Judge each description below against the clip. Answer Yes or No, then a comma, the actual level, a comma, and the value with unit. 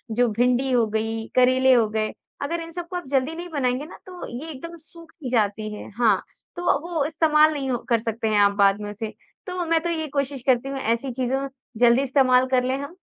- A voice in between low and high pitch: No, very high, 260 Hz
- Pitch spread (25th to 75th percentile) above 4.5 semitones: Yes, average, 5.1 semitones